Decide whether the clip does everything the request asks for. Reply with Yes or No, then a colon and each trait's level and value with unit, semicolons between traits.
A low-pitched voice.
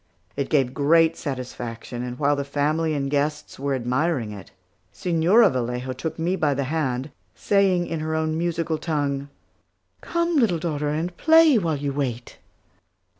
No: medium, 150 Hz